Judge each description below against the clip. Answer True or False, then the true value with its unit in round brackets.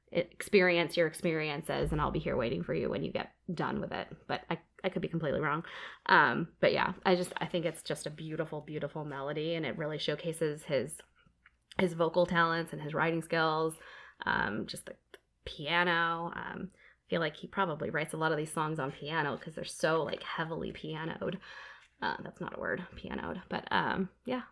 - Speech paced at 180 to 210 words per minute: True (200 wpm)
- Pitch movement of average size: False (2.3 semitones)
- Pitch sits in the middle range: True (165 Hz)